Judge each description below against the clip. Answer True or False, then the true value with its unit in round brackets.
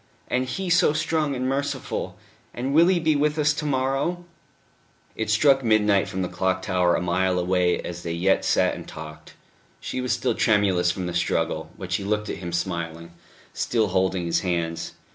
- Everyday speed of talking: True (185 wpm)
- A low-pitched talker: True (100 Hz)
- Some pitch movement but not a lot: False (7.3 semitones)